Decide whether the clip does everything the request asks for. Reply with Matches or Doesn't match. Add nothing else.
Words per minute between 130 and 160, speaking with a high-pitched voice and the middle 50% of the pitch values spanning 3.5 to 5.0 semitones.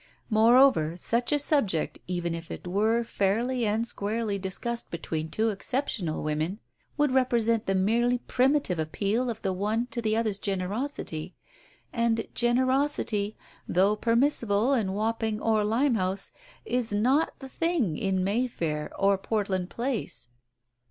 Matches